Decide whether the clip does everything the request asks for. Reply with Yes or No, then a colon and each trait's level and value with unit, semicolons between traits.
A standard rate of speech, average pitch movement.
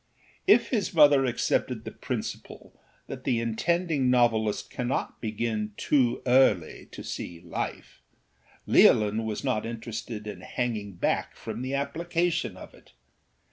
No: slow, 130 wpm; average, 4.5 semitones